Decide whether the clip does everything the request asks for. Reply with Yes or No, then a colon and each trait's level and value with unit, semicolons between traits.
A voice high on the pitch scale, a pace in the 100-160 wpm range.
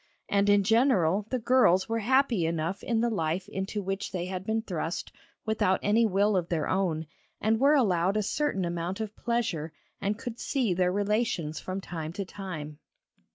No: high, 195 Hz; average, 180 wpm